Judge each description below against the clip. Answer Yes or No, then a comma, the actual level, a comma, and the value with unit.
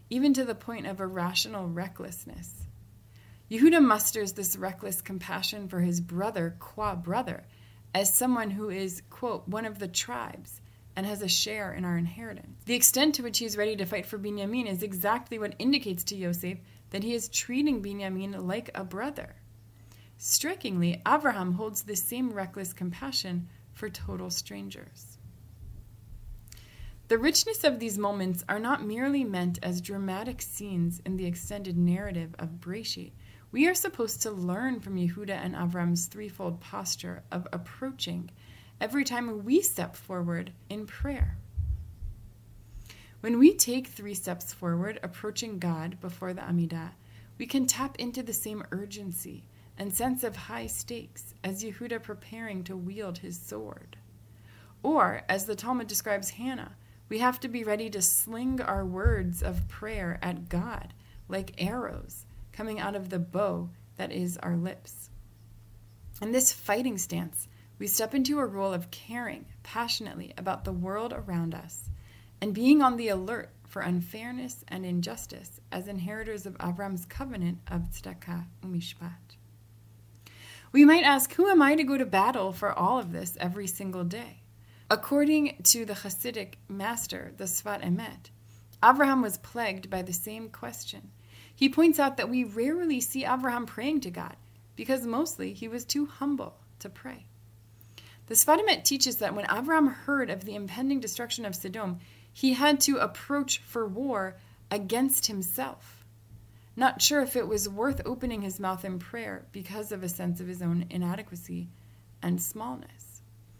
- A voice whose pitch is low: No, high, 190 Hz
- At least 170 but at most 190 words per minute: No, average, 155 wpm